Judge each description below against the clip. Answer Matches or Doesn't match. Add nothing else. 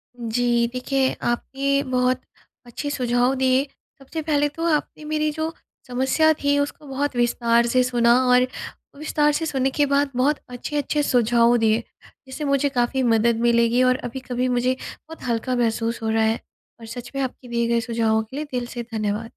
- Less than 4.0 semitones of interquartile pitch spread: Matches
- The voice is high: Matches